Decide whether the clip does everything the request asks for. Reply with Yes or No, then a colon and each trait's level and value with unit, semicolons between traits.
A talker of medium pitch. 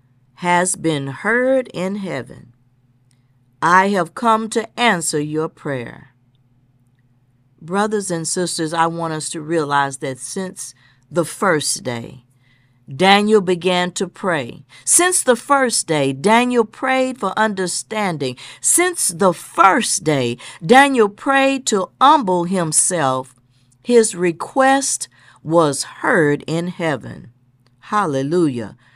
Yes: medium, 165 Hz